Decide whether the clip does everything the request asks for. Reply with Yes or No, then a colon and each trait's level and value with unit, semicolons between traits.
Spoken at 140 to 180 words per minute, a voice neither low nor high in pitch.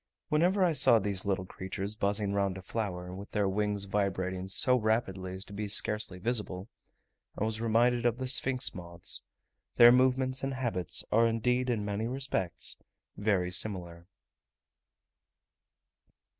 No: average, 145 wpm; low, 105 Hz